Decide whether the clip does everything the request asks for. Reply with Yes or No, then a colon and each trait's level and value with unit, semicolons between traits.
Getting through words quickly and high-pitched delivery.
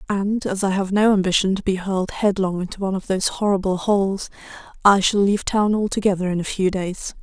Yes: fast, 210 wpm; high, 195 Hz